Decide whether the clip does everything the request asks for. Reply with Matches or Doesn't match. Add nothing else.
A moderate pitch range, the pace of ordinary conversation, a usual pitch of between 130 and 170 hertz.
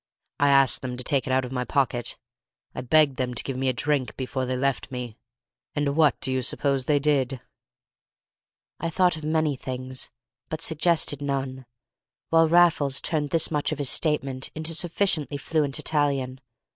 Matches